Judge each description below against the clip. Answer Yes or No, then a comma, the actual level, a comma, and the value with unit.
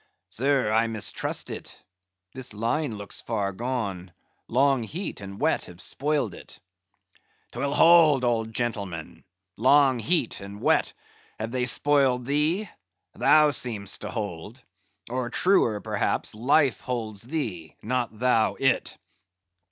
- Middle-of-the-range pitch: No, low, 120 Hz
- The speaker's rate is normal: No, slow, 125 wpm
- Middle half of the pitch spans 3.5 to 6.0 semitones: Yes, average, 4.6 semitones